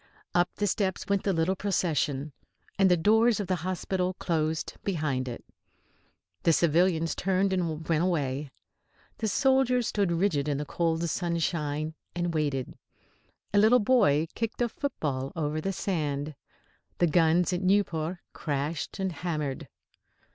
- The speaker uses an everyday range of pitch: Yes, average, 4.0 semitones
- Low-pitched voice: No, medium, 170 Hz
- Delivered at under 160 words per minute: Yes, average, 140 wpm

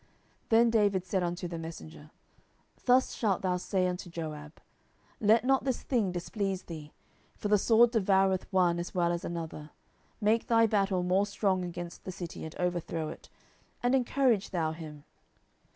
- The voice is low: No, medium, 185 Hz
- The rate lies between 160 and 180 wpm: Yes, average, 165 wpm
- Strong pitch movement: No, average, 3.7 semitones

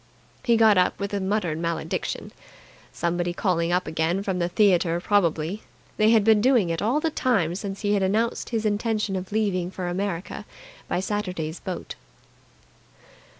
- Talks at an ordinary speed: Yes, average, 160 wpm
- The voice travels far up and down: No, average, 3.4 semitones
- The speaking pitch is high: Yes, high, 195 Hz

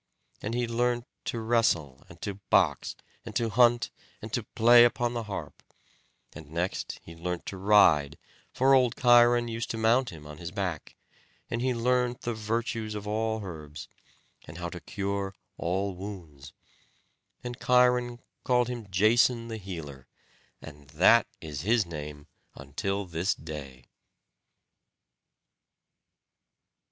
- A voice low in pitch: Yes, low, 105 Hz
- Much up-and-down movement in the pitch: Yes, wide, 6.1 semitones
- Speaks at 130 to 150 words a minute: Yes, average, 140 wpm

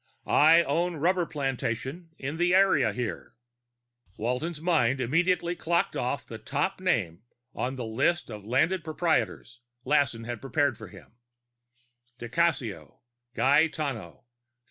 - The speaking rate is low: Yes, slow, 120 wpm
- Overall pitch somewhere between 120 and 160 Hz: Yes, medium, 140 Hz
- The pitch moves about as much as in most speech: No, wide, 6.2 semitones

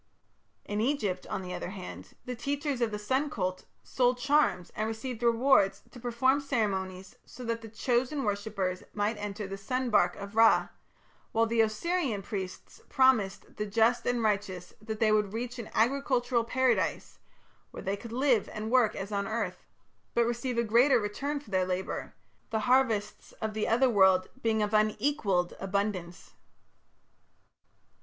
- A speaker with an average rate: Yes, average, 155 wpm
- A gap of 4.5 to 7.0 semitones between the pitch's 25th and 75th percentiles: No, average, 3.6 semitones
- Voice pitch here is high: Yes, high, 220 Hz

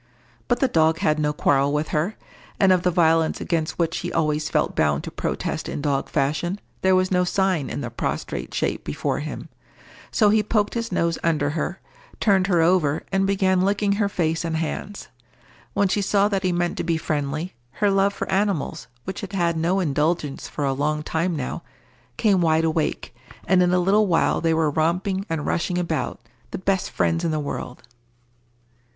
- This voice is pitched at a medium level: Yes, medium, 170 Hz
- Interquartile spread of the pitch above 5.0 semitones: No, average, 3.5 semitones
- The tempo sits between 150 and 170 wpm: No, average, 195 wpm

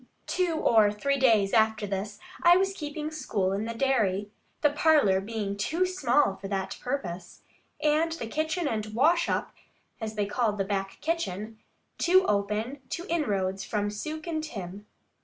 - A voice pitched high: Yes, high, 225 Hz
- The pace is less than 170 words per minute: Yes, average, 160 wpm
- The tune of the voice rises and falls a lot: Yes, wide, 7.2 semitones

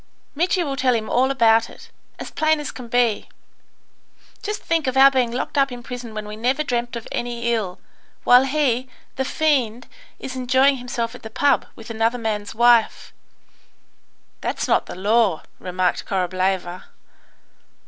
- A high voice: Yes, high, 240 Hz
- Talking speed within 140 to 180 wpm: Yes, average, 160 wpm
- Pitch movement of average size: Yes, average, 3.1 semitones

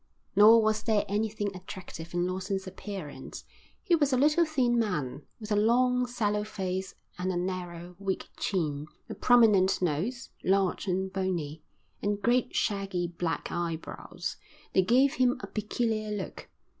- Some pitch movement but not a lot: Yes, average, 3.9 semitones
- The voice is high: Yes, high, 200 Hz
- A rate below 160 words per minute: Yes, average, 145 wpm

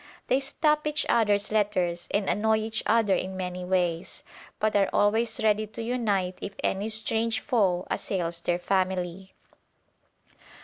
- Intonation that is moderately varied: Yes, average, 3.2 semitones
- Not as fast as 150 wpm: Yes, average, 140 wpm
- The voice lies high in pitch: Yes, high, 205 Hz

